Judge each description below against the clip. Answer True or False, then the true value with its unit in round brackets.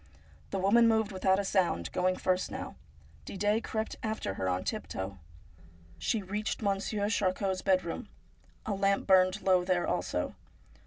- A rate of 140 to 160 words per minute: True (145 wpm)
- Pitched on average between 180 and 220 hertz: True (190 Hz)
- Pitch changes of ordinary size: False (2.1 semitones)